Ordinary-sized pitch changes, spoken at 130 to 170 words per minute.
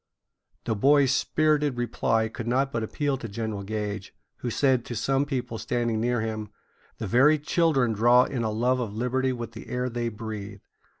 No: average, 3.0 semitones; average, 180 wpm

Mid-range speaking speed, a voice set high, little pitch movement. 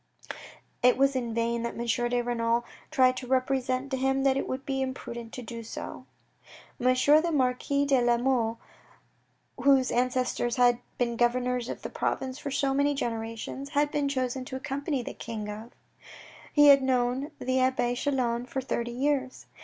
Yes: average, 170 wpm; very high, 255 Hz; narrow, 2.0 semitones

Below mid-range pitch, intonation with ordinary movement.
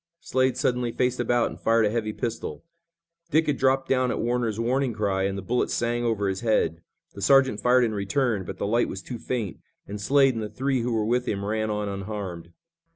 Yes: low, 115 Hz; average, 3.4 semitones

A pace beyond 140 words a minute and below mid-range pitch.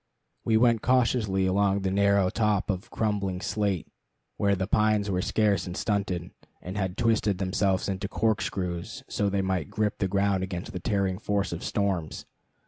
Yes: average, 165 wpm; low, 100 Hz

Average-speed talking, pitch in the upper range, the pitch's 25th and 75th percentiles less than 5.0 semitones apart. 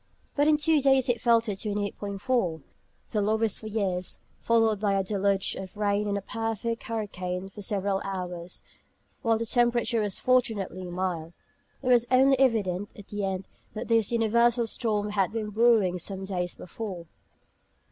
Yes: average, 160 wpm; high, 210 Hz; average, 3.2 semitones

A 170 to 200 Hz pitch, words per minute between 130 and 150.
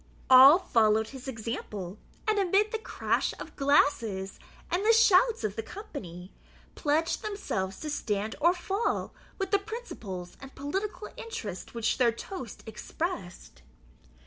No: very high, 275 Hz; slow, 135 wpm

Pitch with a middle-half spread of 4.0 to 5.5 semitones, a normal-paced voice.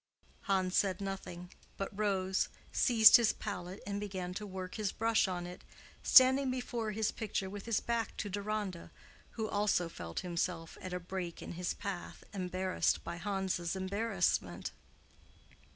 No: average, 2.8 semitones; average, 150 wpm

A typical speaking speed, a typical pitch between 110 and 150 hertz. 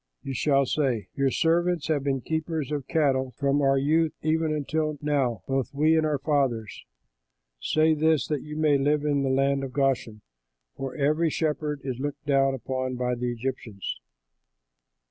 Yes: average, 165 wpm; medium, 140 Hz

